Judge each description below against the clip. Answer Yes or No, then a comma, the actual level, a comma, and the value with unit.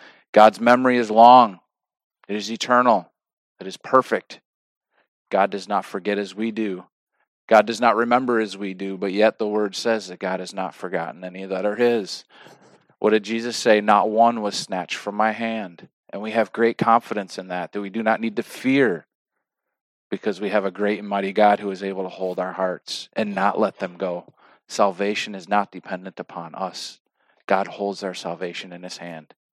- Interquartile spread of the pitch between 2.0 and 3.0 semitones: Yes, narrow, 2.6 semitones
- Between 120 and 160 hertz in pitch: No, low, 105 Hz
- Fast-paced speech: Yes, fast, 195 wpm